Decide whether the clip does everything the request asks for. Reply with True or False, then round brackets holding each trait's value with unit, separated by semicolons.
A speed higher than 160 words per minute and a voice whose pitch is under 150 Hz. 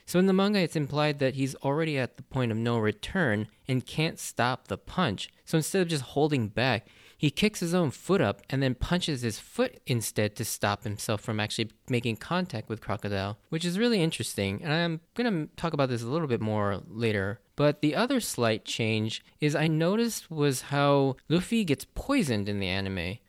True (205 wpm; 135 Hz)